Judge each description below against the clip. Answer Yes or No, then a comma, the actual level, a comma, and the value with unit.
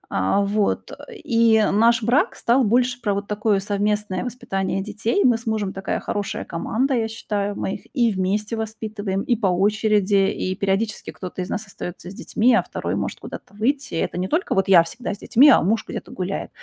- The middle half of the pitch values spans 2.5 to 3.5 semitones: Yes, average, 2.9 semitones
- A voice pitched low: No, high, 210 Hz